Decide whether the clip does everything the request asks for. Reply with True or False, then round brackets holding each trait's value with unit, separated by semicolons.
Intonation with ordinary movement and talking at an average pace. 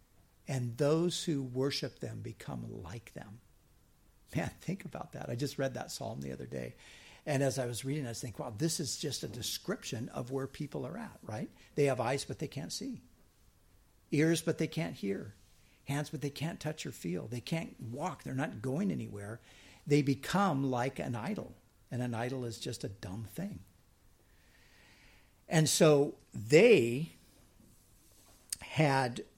False (6.6 semitones; 170 wpm)